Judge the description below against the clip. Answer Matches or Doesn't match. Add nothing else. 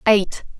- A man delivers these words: Doesn't match